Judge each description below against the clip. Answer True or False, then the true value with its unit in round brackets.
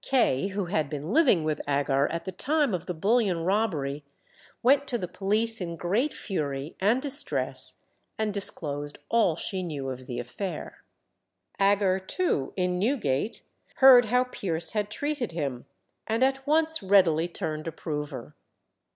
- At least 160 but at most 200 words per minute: False (150 wpm)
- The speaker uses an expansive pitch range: True (6.9 semitones)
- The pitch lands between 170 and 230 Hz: True (190 Hz)